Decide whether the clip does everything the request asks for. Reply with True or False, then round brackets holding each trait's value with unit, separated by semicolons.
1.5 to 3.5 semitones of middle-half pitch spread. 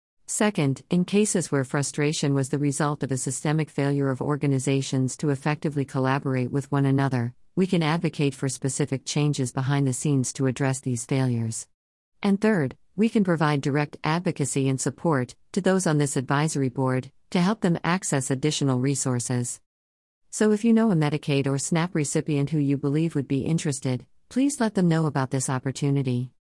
True (3.0 semitones)